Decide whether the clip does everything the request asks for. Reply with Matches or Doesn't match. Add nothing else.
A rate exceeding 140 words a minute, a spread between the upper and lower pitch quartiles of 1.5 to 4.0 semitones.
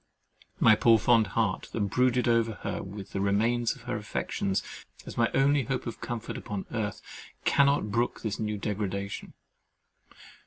Matches